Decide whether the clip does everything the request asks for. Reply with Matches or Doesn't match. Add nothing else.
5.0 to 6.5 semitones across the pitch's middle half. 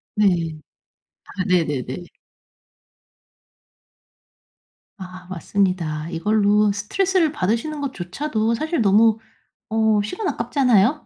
Matches